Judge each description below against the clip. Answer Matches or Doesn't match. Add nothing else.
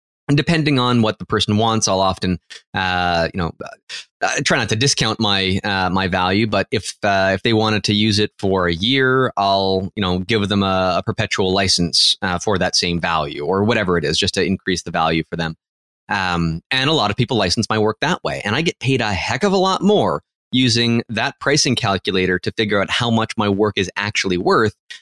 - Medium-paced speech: Doesn't match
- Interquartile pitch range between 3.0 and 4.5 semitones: Matches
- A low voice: Matches